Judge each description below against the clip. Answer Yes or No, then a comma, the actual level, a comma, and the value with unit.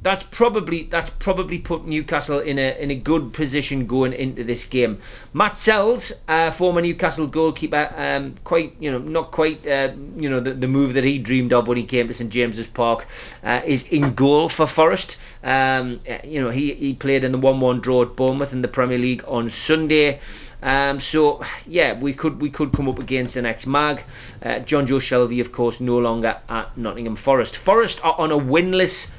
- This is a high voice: No, low, 135 Hz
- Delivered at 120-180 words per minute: No, fast, 205 wpm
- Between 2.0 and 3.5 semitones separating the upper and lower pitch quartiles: No, average, 3.9 semitones